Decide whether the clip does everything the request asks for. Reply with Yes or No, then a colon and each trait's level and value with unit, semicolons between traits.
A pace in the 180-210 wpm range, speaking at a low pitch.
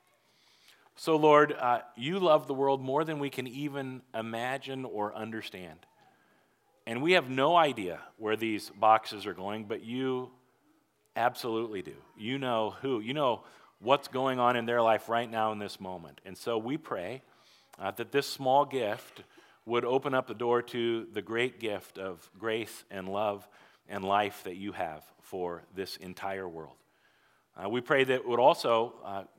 No: average, 170 wpm; low, 115 Hz